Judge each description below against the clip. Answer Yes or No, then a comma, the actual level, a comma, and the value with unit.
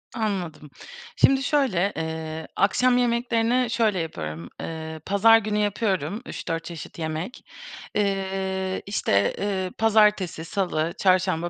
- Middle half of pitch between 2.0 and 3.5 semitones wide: No, average, 4.9 semitones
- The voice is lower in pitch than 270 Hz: Yes, high, 190 Hz